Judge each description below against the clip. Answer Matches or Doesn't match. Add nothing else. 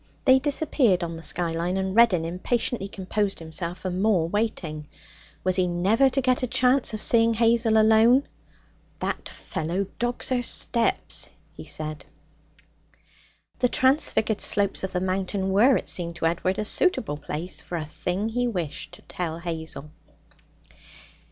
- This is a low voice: Doesn't match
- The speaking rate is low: Doesn't match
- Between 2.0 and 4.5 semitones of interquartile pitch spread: Doesn't match